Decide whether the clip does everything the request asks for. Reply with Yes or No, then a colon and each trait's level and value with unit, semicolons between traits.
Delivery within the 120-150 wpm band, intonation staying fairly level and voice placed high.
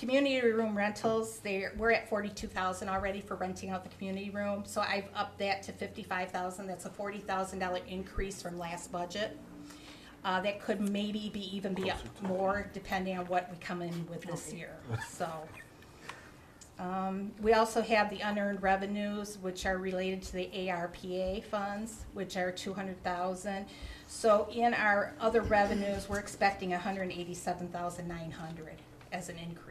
Yes: average, 145 wpm; narrow, 2.0 semitones; high, 195 Hz